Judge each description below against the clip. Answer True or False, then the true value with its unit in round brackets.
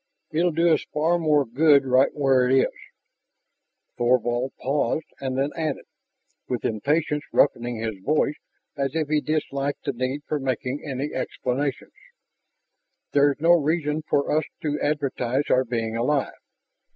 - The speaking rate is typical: True (145 wpm)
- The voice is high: False (140 Hz)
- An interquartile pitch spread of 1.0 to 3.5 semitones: True (2.9 semitones)